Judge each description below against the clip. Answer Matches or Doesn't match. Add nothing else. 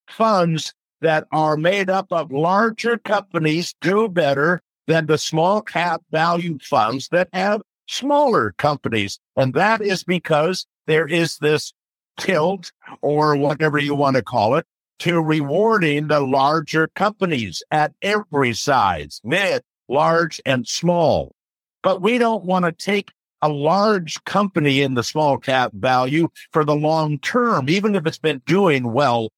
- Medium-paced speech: Matches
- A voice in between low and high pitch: Matches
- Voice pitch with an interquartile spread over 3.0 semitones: Matches